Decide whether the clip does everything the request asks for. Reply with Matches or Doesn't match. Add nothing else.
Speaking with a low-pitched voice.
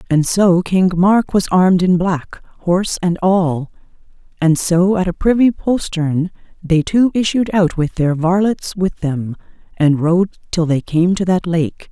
Doesn't match